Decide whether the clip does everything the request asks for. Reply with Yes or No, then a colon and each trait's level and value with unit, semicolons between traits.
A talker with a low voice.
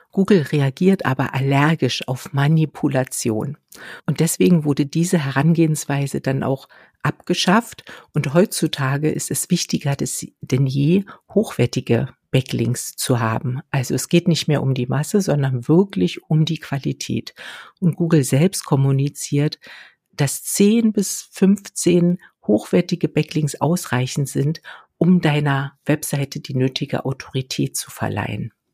No: medium, 145 Hz